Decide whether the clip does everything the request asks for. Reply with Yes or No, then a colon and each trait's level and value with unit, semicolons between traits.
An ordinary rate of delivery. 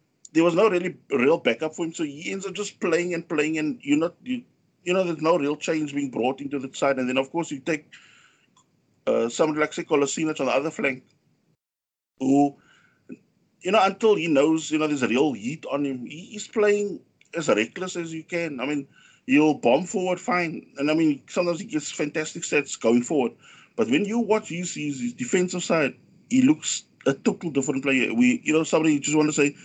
No: fast, 215 wpm